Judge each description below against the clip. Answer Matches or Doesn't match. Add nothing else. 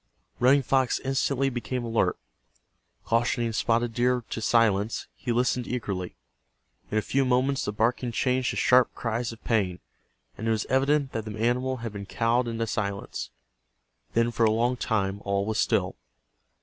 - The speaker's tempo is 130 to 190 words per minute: Matches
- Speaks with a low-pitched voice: Matches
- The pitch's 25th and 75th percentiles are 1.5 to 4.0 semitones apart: Matches